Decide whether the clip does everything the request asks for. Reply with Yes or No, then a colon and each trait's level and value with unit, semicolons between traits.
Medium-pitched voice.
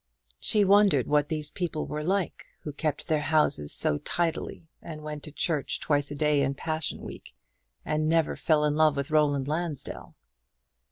Yes: medium, 150 Hz